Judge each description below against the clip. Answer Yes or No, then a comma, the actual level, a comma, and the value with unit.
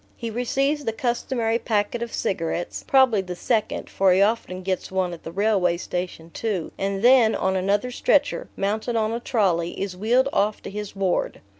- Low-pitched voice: No, high, 205 Hz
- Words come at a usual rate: Yes, average, 180 wpm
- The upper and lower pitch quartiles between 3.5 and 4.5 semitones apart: Yes, average, 3.9 semitones